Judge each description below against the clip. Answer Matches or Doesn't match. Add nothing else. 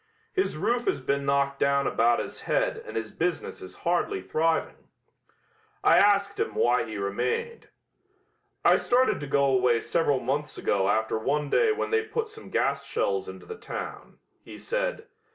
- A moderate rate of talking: Matches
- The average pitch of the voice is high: Doesn't match